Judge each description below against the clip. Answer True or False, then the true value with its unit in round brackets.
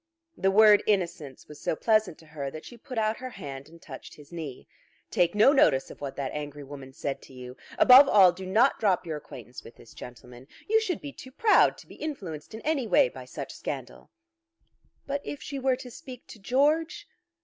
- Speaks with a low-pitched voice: False (190 Hz)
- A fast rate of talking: True (210 wpm)